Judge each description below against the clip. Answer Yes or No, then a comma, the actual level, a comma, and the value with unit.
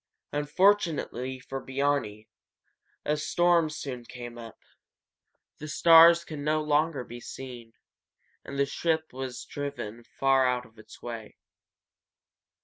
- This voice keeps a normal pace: No, slow, 120 wpm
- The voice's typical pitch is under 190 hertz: Yes, medium, 140 Hz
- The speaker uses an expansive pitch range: No, average, 4.0 semitones